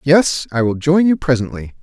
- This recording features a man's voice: Yes, male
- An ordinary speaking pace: Yes, average, 195 wpm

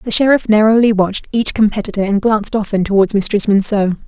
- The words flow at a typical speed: Yes, average, 175 wpm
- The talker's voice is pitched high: Yes, high, 210 Hz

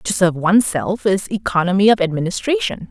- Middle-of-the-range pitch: No, high, 195 Hz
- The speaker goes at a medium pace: Yes, average, 145 wpm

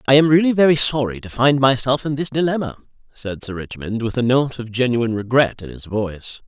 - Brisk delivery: Yes, fast, 215 wpm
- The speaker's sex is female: No, male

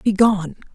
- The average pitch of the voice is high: Yes, high, 200 Hz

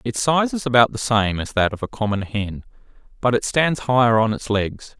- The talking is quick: Yes, fast, 230 wpm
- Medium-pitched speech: No, low, 120 Hz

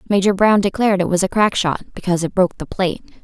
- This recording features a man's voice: No, female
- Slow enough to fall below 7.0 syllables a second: No, 7.3 syllables/s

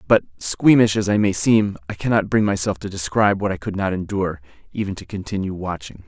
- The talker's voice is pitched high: No, low, 100 Hz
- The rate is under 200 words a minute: No, fast, 205 wpm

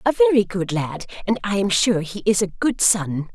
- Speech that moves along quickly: Yes, fast, 235 wpm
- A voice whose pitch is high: Yes, high, 195 Hz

